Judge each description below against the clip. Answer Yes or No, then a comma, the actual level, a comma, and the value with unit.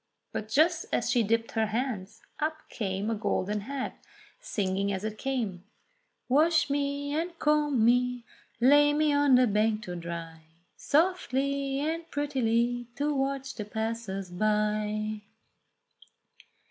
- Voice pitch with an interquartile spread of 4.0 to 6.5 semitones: Yes, average, 5.2 semitones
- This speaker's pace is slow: Yes, slow, 130 wpm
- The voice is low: No, high, 240 Hz